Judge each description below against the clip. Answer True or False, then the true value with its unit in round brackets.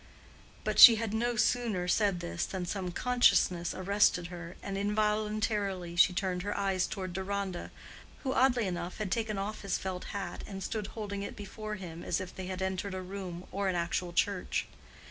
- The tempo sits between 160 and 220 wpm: True (185 wpm)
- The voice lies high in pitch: True (195 Hz)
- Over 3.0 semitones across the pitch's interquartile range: False (2.7 semitones)